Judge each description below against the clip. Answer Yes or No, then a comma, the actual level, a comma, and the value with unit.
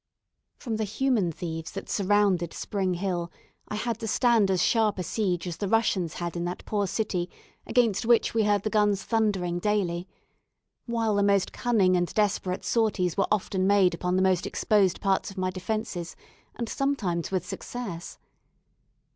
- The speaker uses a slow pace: No, average, 170 wpm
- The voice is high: Yes, high, 195 Hz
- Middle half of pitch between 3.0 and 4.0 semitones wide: Yes, average, 3.3 semitones